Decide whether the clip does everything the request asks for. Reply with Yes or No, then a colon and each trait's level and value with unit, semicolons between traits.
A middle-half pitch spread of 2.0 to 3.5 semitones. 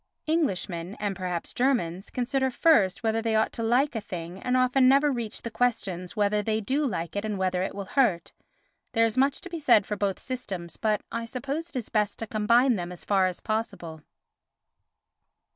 No: average, 5.0 semitones